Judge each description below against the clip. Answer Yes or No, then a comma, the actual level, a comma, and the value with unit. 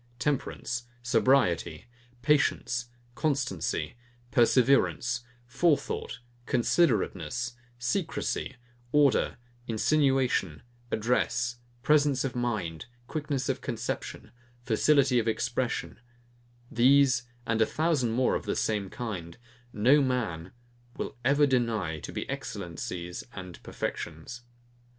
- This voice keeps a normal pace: No, slow, 95 wpm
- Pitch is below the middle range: Yes, low, 120 Hz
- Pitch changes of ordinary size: Yes, average, 3.7 semitones